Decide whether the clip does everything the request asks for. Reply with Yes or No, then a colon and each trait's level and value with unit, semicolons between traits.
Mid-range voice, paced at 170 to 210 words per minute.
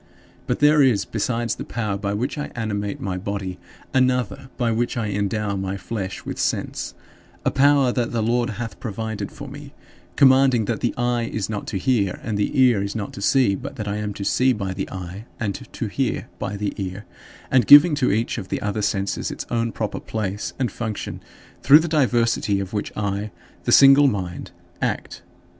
No: low, 110 Hz; average, 195 wpm